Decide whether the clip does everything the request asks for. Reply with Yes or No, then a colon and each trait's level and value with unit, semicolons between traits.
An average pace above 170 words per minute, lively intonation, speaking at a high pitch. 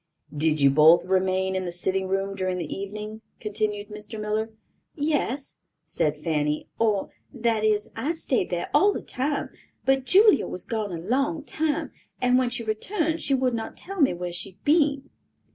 Yes: average, 180 wpm; wide, 6.3 semitones; high, 215 Hz